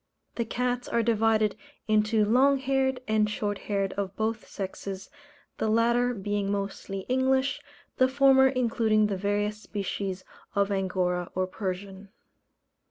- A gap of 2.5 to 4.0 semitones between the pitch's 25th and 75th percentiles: Yes, average, 3.7 semitones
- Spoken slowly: Yes, slow, 130 wpm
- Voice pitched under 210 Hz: No, high, 215 Hz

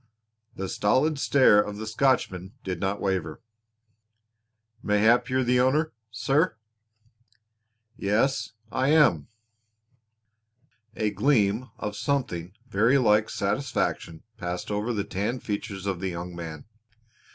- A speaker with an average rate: No, slow, 115 wpm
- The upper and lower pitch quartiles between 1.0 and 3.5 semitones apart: No, average, 5.1 semitones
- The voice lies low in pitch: Yes, low, 105 Hz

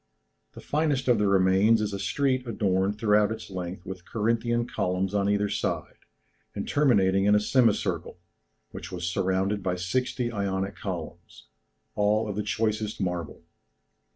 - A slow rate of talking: No, average, 150 wpm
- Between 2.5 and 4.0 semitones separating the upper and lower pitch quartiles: Yes, average, 3.1 semitones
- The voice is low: Yes, low, 105 Hz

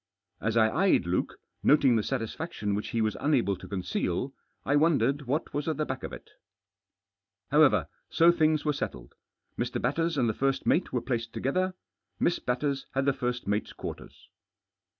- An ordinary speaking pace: Yes, average, 170 wpm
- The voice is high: No, low, 135 Hz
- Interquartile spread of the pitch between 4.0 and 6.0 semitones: Yes, average, 5.0 semitones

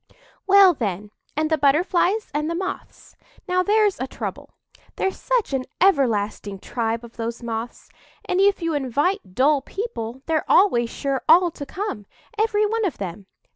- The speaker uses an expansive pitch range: Yes, wide, 8.5 semitones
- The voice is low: No, very high, 305 Hz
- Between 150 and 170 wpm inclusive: Yes, average, 160 wpm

